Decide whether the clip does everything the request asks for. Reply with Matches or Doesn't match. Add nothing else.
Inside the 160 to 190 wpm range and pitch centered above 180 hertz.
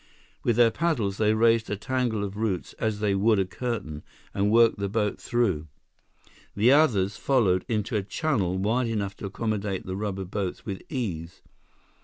Doesn't match